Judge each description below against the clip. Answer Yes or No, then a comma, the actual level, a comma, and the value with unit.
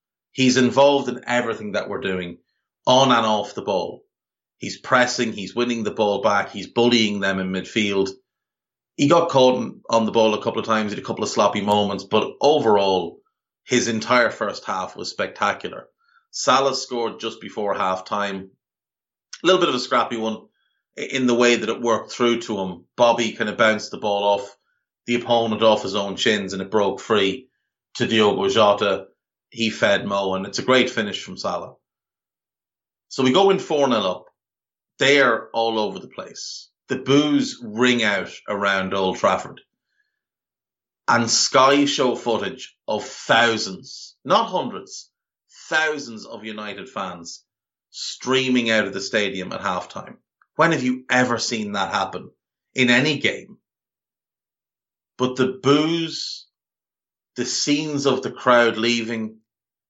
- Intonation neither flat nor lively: Yes, average, 3.4 semitones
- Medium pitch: No, low, 115 Hz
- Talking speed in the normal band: Yes, average, 160 wpm